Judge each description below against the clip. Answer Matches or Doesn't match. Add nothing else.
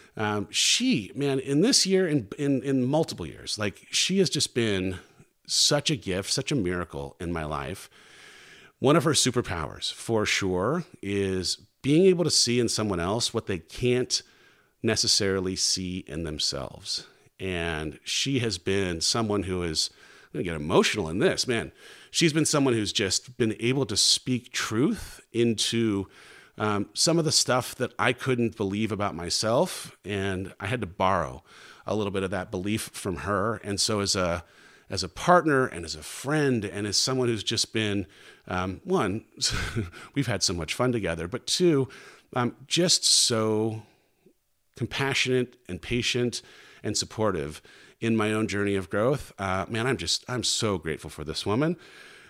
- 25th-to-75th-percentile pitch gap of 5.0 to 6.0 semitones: Matches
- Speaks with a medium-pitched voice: Doesn't match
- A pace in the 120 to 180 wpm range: Matches